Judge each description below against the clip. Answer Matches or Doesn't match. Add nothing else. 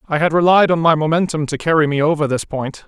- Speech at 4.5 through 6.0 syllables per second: Doesn't match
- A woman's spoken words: Doesn't match